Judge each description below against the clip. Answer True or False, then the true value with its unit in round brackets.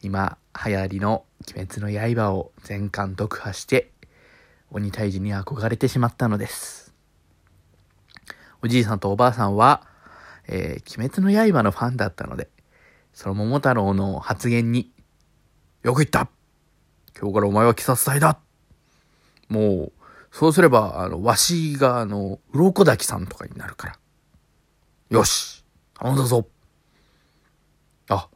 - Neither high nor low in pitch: False (105 Hz)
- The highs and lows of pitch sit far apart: False (4.2 semitones)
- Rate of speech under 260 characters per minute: True (245 characters per minute)